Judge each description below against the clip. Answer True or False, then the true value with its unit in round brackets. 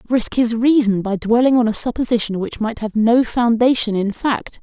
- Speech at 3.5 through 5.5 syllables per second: True (5.0 syllables/s)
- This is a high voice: True (230 Hz)